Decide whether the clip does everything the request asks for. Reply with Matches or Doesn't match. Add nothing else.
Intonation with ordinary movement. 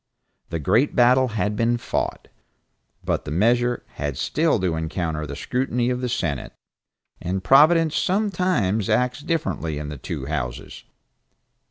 Doesn't match